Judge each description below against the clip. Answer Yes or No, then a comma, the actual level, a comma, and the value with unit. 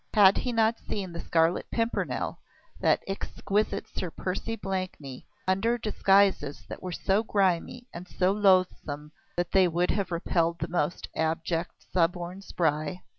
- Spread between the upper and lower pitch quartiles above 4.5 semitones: No, average, 2.9 semitones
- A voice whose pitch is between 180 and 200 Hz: Yes, medium, 185 Hz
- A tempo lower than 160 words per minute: Yes, average, 140 wpm